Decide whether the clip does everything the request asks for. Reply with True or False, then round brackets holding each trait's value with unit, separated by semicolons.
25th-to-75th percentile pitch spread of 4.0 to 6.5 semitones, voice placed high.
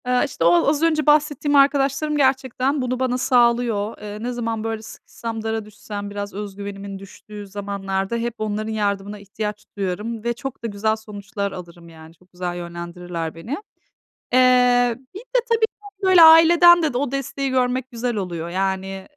True (4.6 semitones; 225 Hz)